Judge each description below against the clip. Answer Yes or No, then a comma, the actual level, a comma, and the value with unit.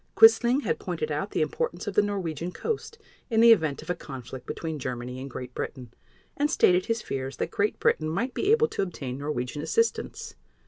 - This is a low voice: No, medium, 170 Hz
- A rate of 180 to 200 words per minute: Yes, average, 195 wpm